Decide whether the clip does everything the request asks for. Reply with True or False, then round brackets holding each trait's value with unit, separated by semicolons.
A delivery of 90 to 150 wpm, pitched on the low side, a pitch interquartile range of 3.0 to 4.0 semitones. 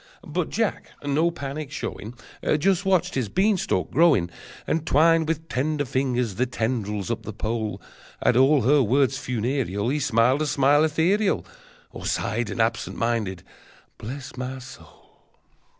False (145 wpm; 130 Hz; 5.0 semitones)